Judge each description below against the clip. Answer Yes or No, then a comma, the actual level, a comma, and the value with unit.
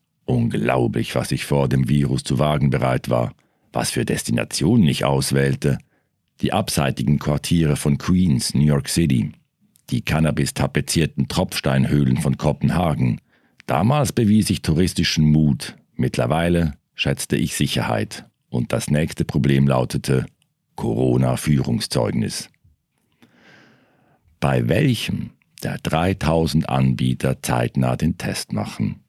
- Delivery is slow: Yes, slow, 110 wpm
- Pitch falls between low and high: No, very low, 70 Hz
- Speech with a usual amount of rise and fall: Yes, average, 3.4 semitones